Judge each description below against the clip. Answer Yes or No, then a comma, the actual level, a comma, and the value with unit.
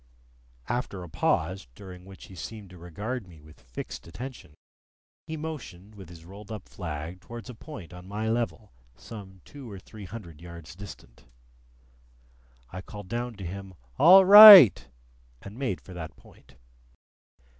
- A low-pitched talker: Yes, very low, 95 Hz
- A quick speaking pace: No, average, 155 wpm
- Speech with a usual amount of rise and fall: Yes, average, 4.6 semitones